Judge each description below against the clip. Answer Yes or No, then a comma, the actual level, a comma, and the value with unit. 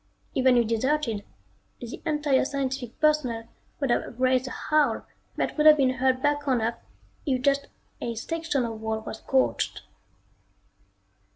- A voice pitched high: Yes, very high, 260 Hz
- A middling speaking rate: Yes, average, 150 wpm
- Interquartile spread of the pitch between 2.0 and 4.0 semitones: Yes, average, 3.6 semitones